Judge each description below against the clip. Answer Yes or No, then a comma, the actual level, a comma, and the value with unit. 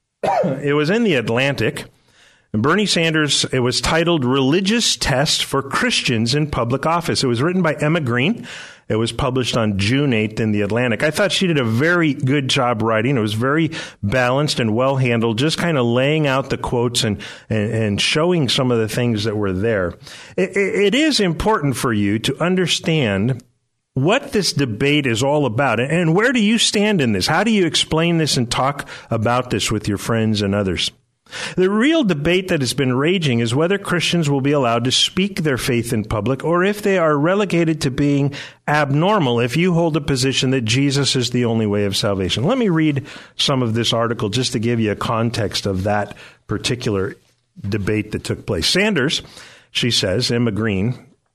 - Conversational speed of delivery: Yes, average, 195 wpm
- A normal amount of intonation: No, wide, 5.7 semitones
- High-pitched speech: No, low, 135 Hz